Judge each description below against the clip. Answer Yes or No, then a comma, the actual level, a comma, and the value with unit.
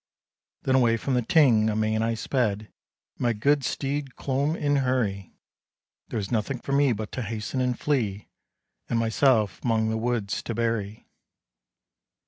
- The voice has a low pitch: Yes, low, 115 Hz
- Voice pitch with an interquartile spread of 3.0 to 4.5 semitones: Yes, average, 3.4 semitones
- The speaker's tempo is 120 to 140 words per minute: No, average, 155 wpm